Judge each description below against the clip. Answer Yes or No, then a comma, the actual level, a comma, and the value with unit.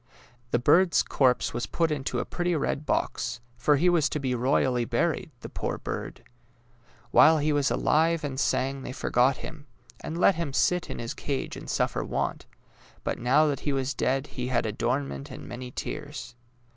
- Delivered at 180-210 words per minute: Yes, average, 185 wpm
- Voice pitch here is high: No, medium, 140 Hz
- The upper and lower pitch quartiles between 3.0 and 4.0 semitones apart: Yes, average, 3.5 semitones